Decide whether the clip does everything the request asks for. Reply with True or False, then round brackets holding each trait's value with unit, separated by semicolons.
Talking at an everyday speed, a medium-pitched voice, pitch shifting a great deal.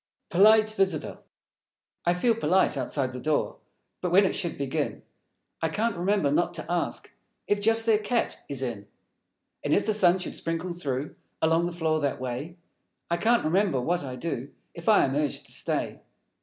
True (180 wpm; 170 Hz; 5.8 semitones)